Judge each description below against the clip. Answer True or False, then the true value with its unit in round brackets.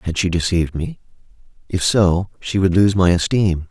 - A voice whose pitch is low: True (90 Hz)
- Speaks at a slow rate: False (180 wpm)